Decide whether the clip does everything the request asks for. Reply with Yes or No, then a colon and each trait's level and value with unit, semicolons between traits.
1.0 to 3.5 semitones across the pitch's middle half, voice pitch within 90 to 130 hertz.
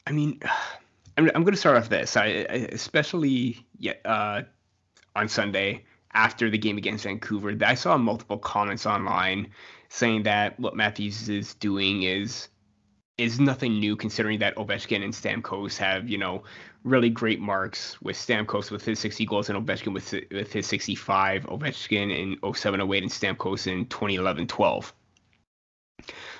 Yes: narrow, 2.4 semitones; low, 105 Hz